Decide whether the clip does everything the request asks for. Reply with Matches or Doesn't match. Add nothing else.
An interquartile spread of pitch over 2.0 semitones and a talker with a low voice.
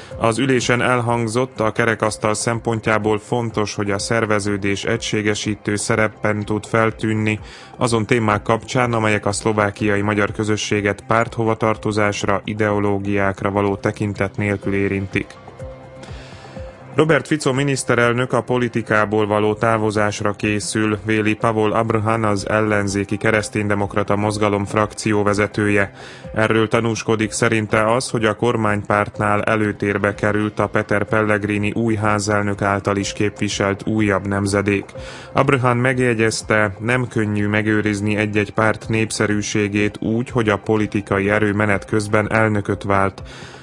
Doesn't match